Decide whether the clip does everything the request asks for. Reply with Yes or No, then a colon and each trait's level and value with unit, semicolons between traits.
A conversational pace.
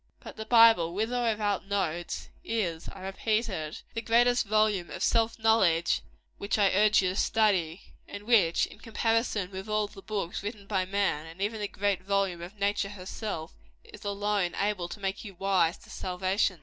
Yes: average, 185 wpm